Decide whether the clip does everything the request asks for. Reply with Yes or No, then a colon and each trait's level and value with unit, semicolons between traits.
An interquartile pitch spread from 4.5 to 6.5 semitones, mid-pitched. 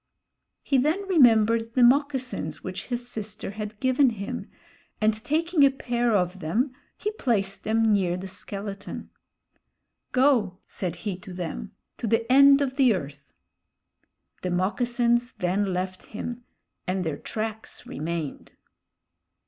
No: average, 5.0 semitones; high, 220 Hz